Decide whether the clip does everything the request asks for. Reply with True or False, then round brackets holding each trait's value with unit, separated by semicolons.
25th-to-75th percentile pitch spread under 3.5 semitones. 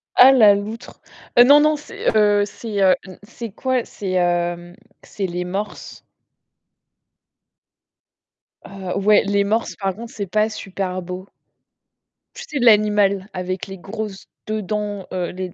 True (2.7 semitones)